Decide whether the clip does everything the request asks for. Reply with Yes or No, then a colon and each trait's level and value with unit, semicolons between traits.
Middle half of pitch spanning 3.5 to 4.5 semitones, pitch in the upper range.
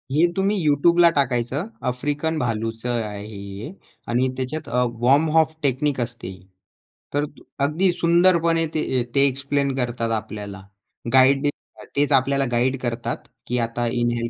No: average, 3.8 semitones; low, 130 Hz